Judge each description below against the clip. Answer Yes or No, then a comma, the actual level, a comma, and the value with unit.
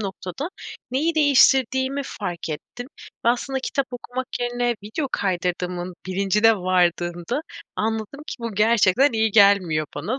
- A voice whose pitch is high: Yes, high, 220 Hz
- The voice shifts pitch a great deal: Yes, wide, 5.8 semitones